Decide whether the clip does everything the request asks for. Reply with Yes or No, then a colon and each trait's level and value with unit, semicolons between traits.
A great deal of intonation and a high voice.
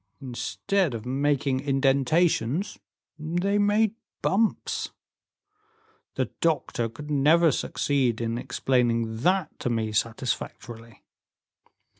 No: wide, 6.1 semitones; low, 135 Hz